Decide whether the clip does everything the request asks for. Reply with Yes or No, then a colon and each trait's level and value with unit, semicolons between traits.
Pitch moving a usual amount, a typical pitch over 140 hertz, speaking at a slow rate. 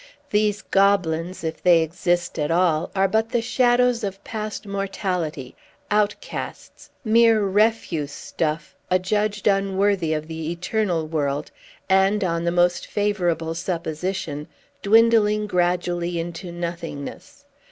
Yes: average, 3.8 semitones; medium, 185 Hz; slow, 115 wpm